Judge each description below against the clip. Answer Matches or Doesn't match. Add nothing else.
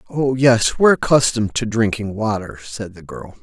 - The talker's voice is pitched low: Matches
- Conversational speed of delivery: Matches